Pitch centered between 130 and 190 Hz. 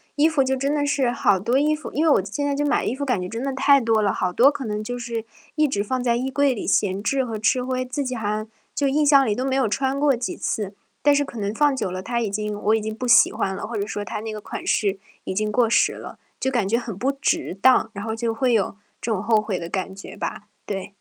No: high, 235 Hz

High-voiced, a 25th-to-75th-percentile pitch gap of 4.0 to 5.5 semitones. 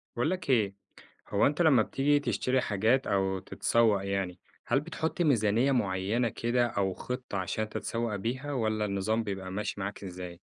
No: low, 110 Hz; average, 4.4 semitones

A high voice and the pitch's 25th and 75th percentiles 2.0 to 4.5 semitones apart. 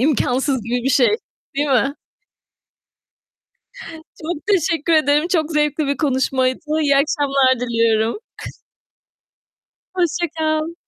Yes: very high, 285 Hz; average, 3.3 semitones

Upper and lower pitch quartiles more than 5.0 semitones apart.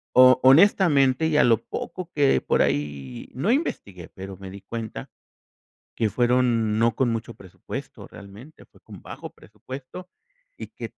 Yes: wide, 5.6 semitones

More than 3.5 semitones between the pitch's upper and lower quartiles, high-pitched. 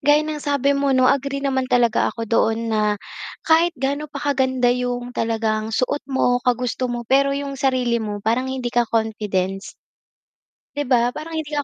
No: average, 3.2 semitones; very high, 255 Hz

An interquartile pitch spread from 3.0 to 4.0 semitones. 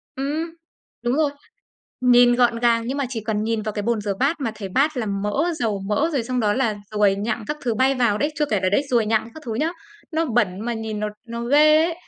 No: average, 4.4 semitones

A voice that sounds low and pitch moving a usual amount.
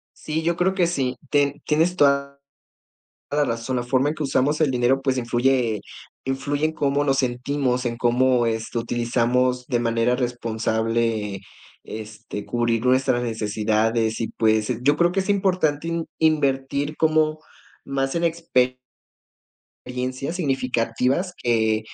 Yes: low, 130 Hz; average, 3.8 semitones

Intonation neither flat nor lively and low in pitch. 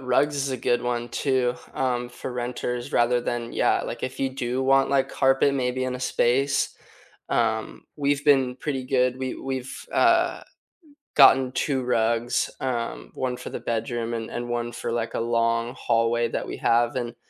No: narrow, 1.9 semitones; low, 125 Hz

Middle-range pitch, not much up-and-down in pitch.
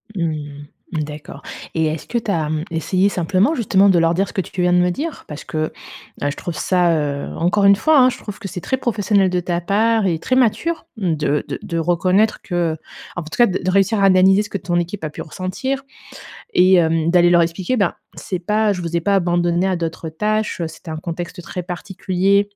No: medium, 180 Hz; average, 3.3 semitones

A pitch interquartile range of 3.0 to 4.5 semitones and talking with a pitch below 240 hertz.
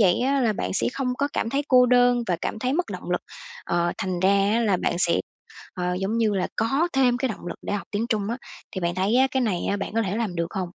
No: average, 5.0 semitones; high, 220 Hz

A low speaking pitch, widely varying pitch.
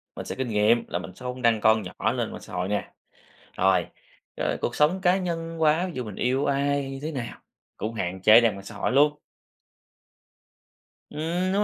Yes: low, 125 Hz; wide, 6.2 semitones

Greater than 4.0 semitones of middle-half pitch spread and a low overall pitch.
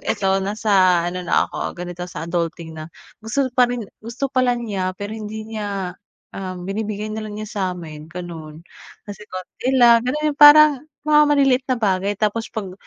No: average, 4.7 semitones; high, 205 Hz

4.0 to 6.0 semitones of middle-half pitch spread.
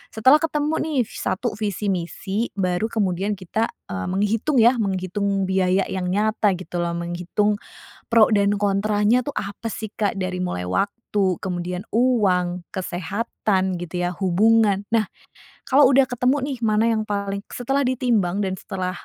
No: average, 3.5 semitones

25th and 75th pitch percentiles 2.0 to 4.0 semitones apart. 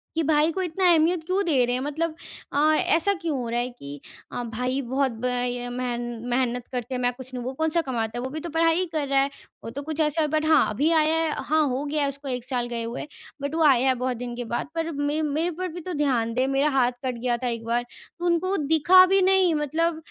No: average, 4.6 semitones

